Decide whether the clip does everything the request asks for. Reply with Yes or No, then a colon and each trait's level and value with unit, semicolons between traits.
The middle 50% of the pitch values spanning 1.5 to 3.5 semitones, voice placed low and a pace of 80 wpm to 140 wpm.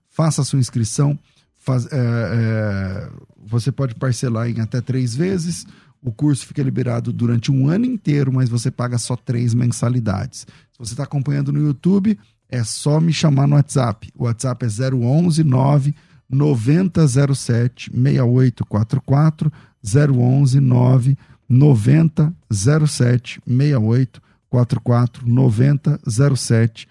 Yes: average, 3.2 semitones; low, 130 Hz; slow, 120 wpm